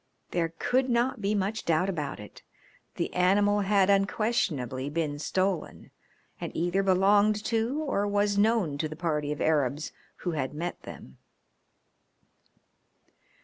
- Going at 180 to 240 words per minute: No, slow, 135 wpm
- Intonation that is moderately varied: Yes, average, 5.0 semitones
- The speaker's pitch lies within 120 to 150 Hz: No, high, 190 Hz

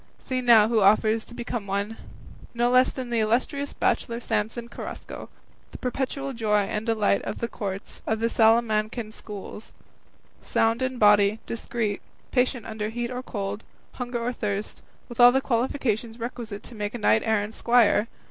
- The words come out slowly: No, average, 165 wpm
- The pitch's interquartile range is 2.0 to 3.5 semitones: Yes, narrow, 2.4 semitones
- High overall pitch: Yes, high, 225 Hz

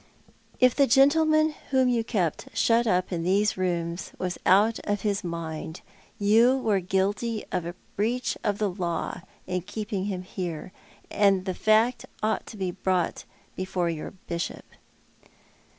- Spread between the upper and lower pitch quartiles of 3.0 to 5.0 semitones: Yes, average, 3.9 semitones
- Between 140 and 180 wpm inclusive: Yes, average, 150 wpm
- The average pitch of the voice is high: Yes, high, 200 Hz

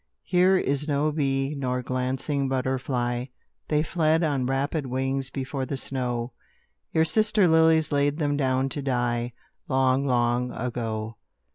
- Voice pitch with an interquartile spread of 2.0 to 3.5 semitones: Yes, average, 2.8 semitones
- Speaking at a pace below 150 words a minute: Yes, slow, 135 wpm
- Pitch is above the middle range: No, low, 135 Hz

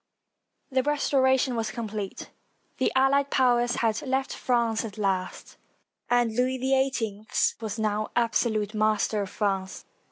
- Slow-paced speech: Yes, slow, 130 wpm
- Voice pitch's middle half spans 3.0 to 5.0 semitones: Yes, average, 3.4 semitones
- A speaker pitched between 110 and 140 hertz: No, high, 230 Hz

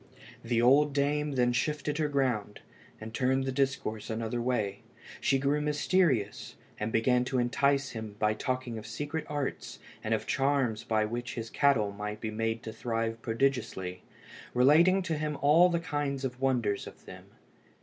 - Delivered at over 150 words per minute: Yes, average, 160 wpm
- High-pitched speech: No, low, 125 Hz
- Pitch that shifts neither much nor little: Yes, average, 4.1 semitones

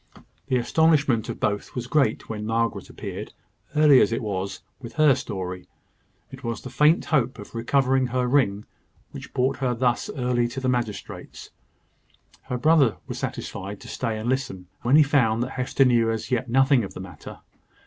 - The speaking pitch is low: Yes, low, 125 Hz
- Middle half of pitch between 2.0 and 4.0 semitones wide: Yes, average, 2.9 semitones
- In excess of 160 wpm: Yes, average, 180 wpm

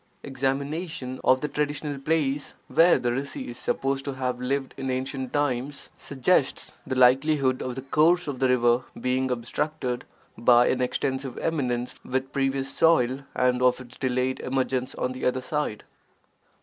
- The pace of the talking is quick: No, average, 155 wpm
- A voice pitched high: No, low, 130 Hz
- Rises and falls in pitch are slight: Yes, narrow, 1.8 semitones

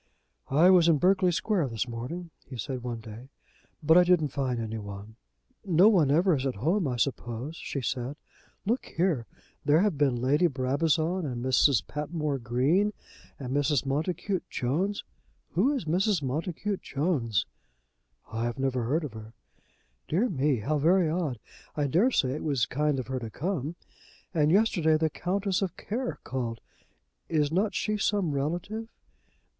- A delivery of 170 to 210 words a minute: No, average, 160 wpm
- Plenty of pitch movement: Yes, wide, 5.7 semitones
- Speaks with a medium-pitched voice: Yes, medium, 150 Hz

